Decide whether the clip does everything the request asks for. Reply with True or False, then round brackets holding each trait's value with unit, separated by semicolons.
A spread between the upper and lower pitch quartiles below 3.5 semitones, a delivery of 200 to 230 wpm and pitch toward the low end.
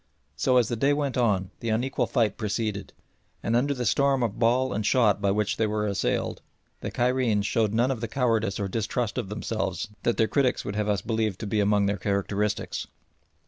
True (3.1 semitones; 205 wpm; 110 Hz)